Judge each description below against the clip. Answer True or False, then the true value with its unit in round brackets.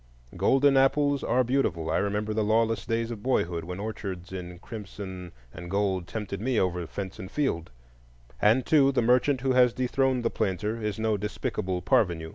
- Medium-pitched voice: False (105 Hz)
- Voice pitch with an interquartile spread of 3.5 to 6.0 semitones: True (5.4 semitones)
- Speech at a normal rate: True (165 wpm)